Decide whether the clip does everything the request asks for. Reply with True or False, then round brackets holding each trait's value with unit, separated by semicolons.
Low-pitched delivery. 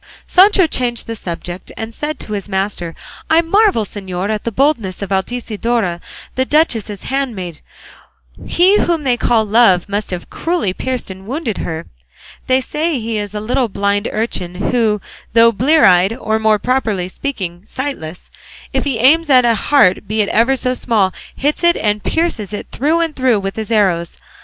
False (225 Hz)